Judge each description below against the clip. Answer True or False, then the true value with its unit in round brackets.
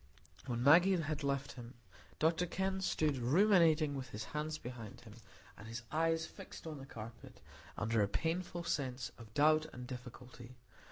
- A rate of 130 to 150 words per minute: False (160 wpm)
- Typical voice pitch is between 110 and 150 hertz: True (140 Hz)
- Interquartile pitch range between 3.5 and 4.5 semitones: False (5.1 semitones)